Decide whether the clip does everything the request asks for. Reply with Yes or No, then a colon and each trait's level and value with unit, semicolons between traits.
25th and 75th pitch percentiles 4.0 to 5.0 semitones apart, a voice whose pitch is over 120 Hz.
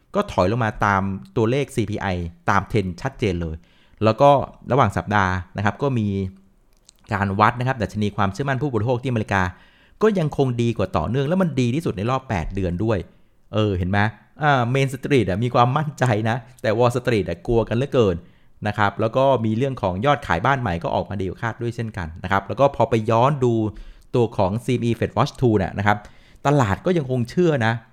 No: average, 4.7 semitones; low, 110 Hz